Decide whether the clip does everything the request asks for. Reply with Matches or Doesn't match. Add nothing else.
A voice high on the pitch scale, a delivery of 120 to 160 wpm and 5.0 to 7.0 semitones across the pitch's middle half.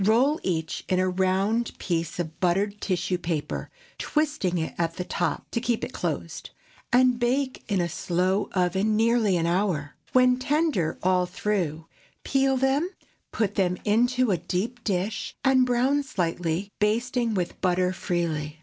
Matches